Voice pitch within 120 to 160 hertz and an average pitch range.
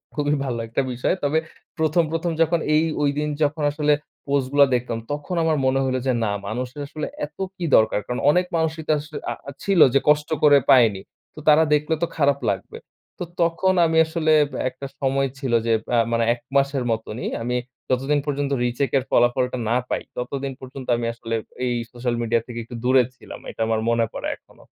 Yes: medium, 140 Hz; average, 3.5 semitones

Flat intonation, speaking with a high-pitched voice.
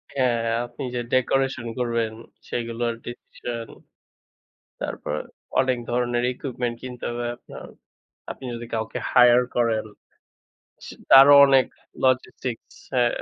No: narrow, 1.6 semitones; low, 120 Hz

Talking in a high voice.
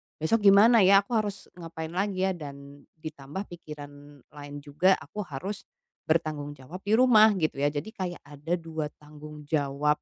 No: medium, 155 Hz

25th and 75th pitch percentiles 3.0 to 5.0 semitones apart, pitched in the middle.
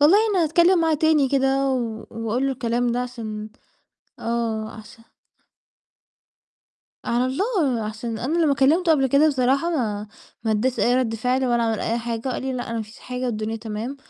No: average, 3.5 semitones; very high, 250 Hz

